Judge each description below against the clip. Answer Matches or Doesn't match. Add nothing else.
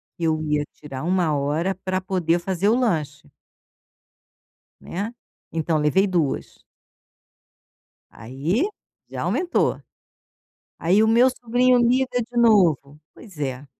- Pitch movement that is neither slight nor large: Doesn't match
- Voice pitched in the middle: Matches